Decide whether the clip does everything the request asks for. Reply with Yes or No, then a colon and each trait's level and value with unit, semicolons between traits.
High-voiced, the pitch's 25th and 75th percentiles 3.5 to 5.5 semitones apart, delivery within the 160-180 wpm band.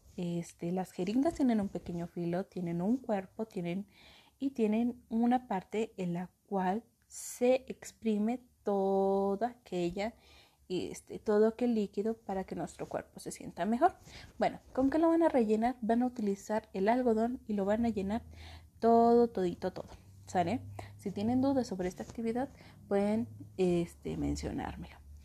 No: high, 205 Hz; average, 4.4 semitones; average, 150 wpm